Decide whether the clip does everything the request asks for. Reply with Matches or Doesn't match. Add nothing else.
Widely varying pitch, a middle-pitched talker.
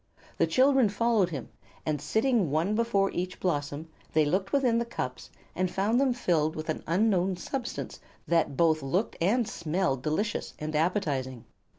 Matches